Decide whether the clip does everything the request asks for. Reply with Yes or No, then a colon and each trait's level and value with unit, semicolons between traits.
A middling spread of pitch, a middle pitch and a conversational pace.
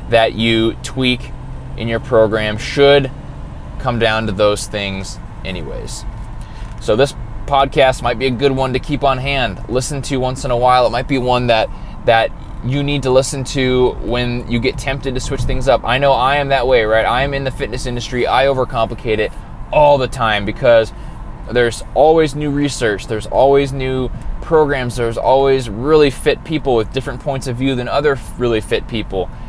No: average, 3.3 semitones; low, 125 Hz; average, 190 wpm